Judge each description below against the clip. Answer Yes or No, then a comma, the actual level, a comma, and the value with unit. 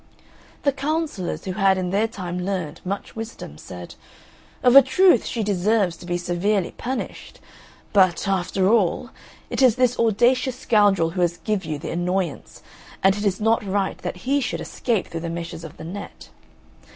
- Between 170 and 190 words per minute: Yes, average, 175 wpm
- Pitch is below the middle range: No, high, 195 Hz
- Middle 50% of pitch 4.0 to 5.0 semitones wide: Yes, average, 4.5 semitones